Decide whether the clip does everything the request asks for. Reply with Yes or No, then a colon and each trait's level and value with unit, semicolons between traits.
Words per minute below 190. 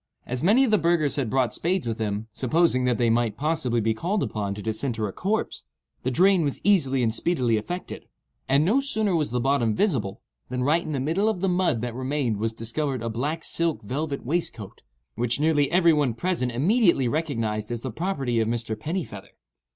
No: average, 200 wpm